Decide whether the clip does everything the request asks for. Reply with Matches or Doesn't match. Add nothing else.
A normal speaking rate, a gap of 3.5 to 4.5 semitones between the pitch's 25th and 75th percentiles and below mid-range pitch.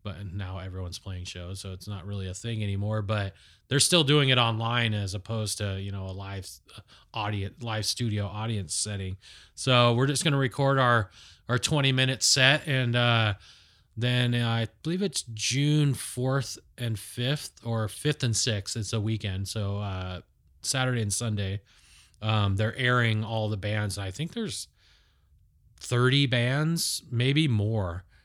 Matches